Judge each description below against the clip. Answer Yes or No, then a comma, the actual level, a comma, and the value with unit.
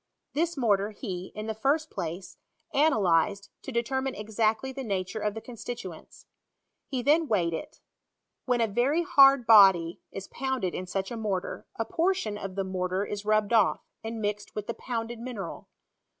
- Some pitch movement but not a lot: Yes, average, 4.5 semitones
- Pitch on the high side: Yes, high, 220 Hz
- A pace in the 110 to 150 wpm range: No, average, 160 wpm